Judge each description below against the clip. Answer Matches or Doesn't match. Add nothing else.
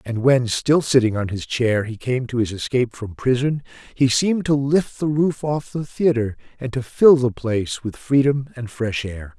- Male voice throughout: Matches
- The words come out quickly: Matches